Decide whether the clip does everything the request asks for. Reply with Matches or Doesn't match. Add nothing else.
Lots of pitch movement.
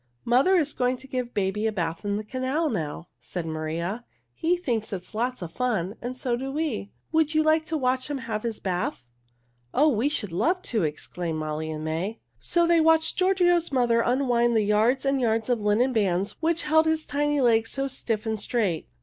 Matches